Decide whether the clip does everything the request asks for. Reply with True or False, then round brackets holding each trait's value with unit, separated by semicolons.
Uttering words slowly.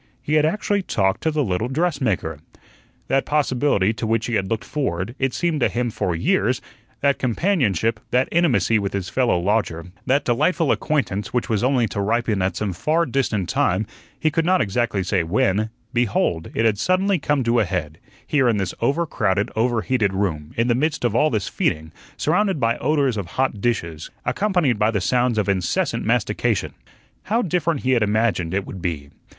False (190 wpm)